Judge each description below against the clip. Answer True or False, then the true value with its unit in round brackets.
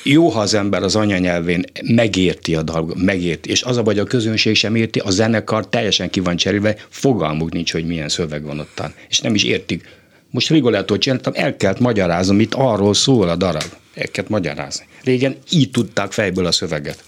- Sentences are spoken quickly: True (185 wpm)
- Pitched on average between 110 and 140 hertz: False (100 Hz)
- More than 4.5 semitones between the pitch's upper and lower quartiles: True (5.0 semitones)